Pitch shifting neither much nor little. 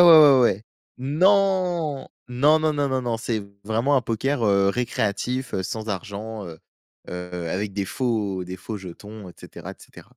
No: wide, 5.8 semitones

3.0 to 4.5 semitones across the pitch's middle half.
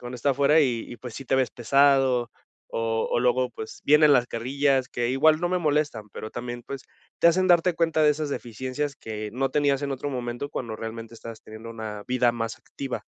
Yes: average, 3.6 semitones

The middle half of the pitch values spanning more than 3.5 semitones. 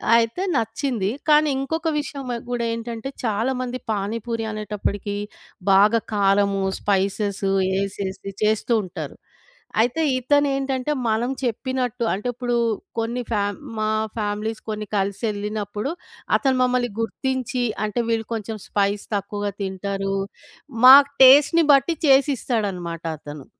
Yes: average, 4.0 semitones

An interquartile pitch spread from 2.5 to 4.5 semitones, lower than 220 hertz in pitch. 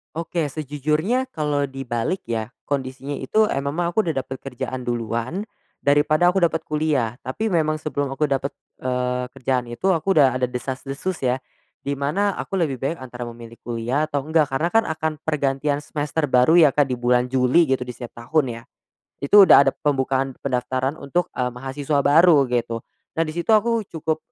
Yes: average, 3.8 semitones; medium, 140 Hz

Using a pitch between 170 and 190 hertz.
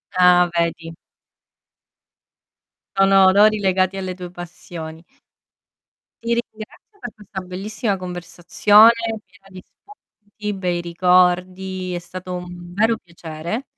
Yes: medium, 185 Hz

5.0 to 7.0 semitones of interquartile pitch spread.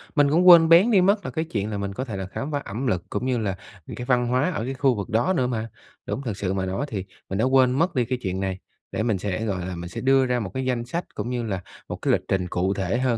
Yes: wide, 5.5 semitones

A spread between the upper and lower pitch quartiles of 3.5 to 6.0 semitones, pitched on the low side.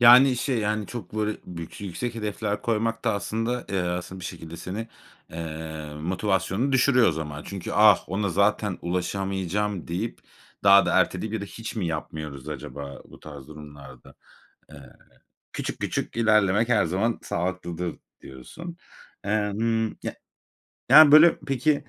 Yes: average, 5.0 semitones; low, 100 Hz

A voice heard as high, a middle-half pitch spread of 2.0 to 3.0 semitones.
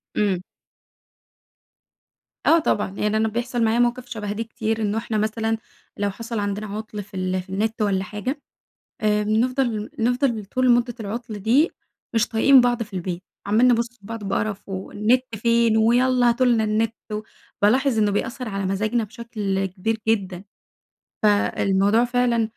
Yes: high, 220 Hz; narrow, 2.5 semitones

